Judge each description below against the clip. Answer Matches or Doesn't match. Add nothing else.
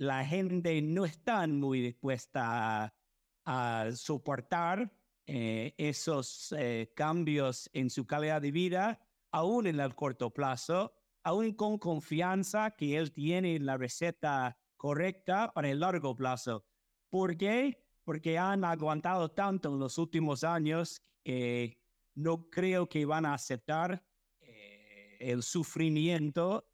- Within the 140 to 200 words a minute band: Doesn't match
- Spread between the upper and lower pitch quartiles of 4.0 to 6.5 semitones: Matches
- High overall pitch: Doesn't match